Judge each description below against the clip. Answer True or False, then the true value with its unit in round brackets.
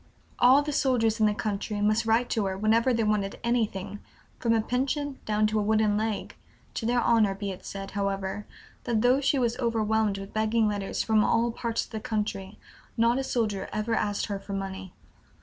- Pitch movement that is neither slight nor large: False (2.3 semitones)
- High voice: True (215 Hz)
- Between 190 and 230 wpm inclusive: True (200 wpm)